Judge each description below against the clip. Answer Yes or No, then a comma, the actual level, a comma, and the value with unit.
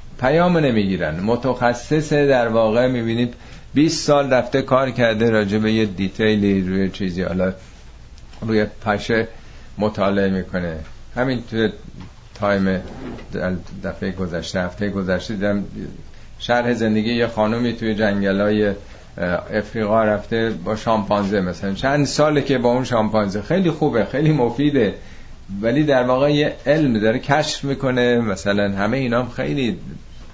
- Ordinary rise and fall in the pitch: Yes, average, 3.9 semitones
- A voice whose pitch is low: Yes, low, 110 Hz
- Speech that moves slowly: No, average, 125 wpm